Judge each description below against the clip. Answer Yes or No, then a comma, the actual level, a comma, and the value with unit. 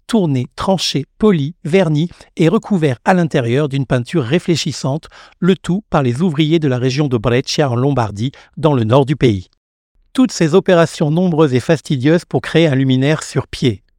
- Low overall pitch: No, medium, 155 Hz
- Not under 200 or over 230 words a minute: No, average, 170 wpm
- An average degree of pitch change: Yes, average, 4.9 semitones